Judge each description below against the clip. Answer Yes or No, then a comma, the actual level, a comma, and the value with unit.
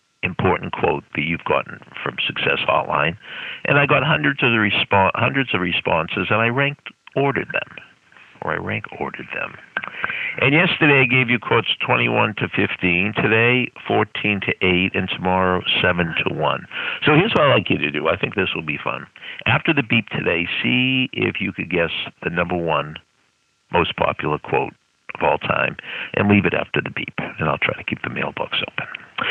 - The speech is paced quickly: No, average, 190 wpm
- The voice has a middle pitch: No, low, 110 Hz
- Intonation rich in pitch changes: Yes, wide, 6.3 semitones